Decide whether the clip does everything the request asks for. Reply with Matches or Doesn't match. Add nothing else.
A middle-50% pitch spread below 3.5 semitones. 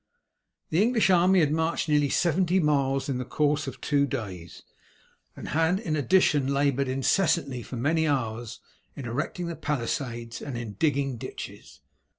Doesn't match